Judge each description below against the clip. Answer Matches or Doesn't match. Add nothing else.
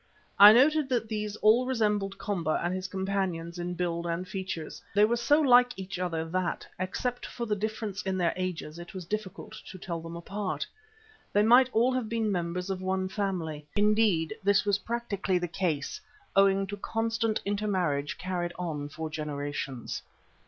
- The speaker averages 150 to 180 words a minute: Matches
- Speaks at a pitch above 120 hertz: Matches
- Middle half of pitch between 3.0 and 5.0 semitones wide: Matches